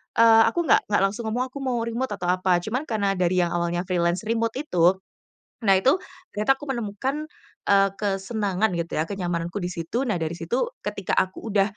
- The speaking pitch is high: Yes, high, 205 Hz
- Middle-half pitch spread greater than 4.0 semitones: Yes, average, 4.6 semitones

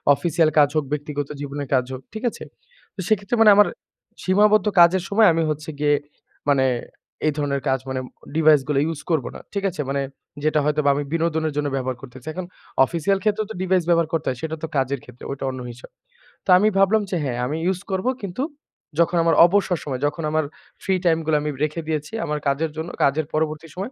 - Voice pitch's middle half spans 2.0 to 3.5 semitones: No, average, 4.1 semitones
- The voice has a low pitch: No, medium, 155 Hz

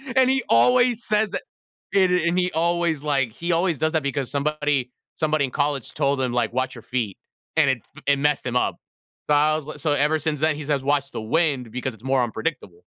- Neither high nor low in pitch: Yes, medium, 145 Hz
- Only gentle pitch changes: No, average, 3.5 semitones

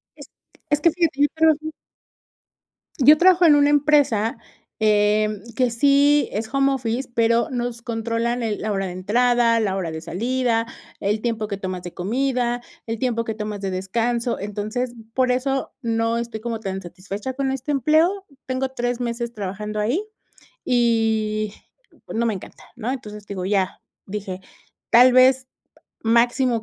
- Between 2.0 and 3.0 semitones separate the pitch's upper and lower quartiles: No, average, 3.6 semitones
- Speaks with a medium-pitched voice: No, high, 235 Hz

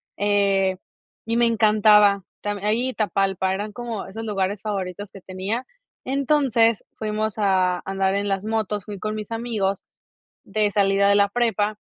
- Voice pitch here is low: No, high, 205 Hz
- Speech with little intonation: Yes, narrow, 2.0 semitones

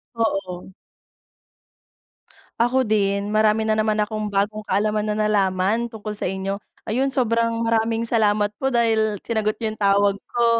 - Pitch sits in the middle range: No, high, 215 Hz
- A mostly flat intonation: Yes, narrow, 1.9 semitones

